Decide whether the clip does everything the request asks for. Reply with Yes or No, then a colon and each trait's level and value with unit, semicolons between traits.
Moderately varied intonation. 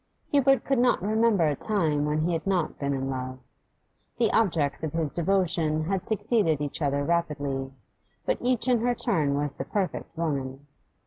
No: wide, 6.3 semitones